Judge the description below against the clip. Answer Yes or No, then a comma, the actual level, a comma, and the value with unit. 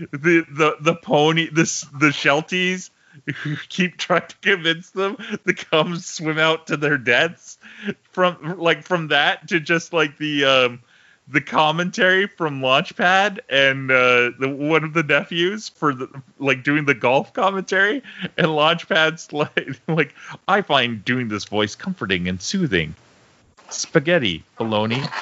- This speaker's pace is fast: No, average, 145 wpm